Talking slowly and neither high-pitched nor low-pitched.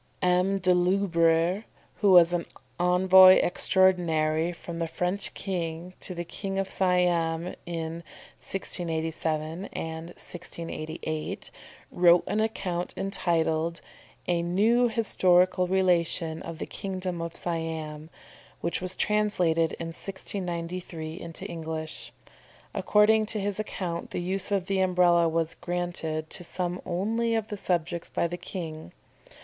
Yes: slow, 125 wpm; medium, 175 Hz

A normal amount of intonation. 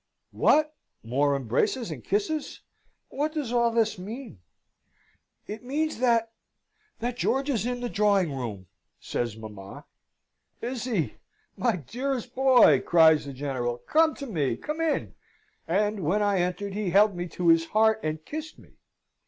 No: wide, 8.1 semitones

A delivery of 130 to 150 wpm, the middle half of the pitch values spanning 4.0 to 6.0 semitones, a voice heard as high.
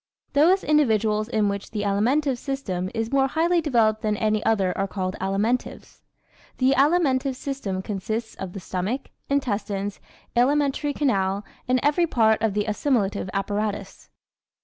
Yes: average, 145 wpm; average, 5.3 semitones; high, 220 Hz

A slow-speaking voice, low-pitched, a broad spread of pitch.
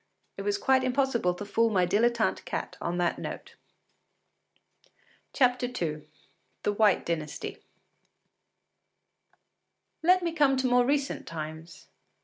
No: slow, 115 wpm; high, 235 Hz; wide, 7.2 semitones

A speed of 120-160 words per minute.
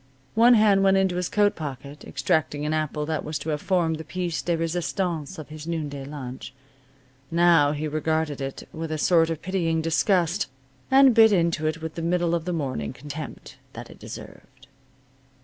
No: average, 185 wpm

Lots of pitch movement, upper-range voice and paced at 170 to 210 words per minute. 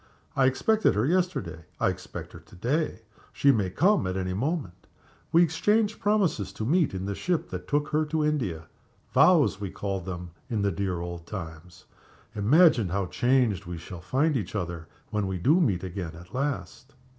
No: wide, 8.7 semitones; low, 105 Hz; average, 180 wpm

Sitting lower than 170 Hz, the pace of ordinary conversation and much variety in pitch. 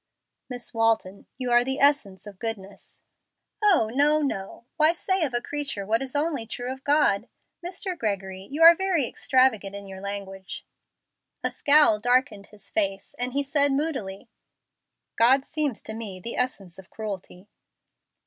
No: high, 240 Hz; average, 160 wpm; wide, 6.1 semitones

